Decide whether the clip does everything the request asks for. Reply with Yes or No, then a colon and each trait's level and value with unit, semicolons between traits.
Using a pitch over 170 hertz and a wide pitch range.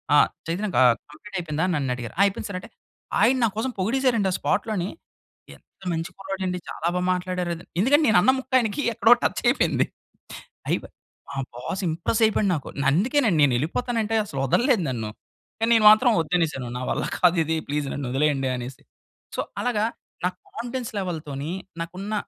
Yes: medium, 185 Hz; wide, 6.6 semitones